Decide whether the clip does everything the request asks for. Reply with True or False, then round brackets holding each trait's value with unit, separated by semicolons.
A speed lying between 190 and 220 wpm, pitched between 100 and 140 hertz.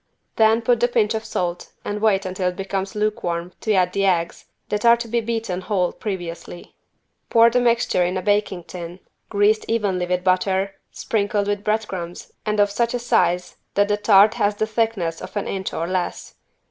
False (195 wpm; 205 Hz)